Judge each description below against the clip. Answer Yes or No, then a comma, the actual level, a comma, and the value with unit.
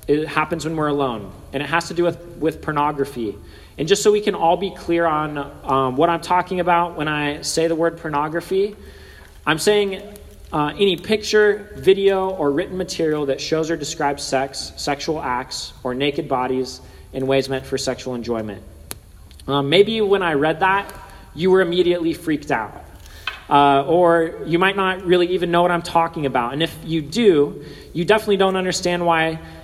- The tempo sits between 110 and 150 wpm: No, average, 180 wpm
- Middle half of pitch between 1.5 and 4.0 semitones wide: No, average, 4.4 semitones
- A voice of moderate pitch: Yes, medium, 160 Hz